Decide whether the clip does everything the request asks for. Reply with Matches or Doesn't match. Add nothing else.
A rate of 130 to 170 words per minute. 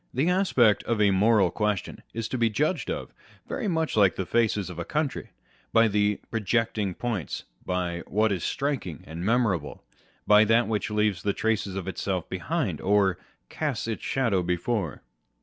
Matches